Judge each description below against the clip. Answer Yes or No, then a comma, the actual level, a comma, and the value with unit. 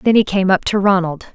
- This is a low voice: No, high, 190 Hz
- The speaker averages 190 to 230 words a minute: No, fast, 265 wpm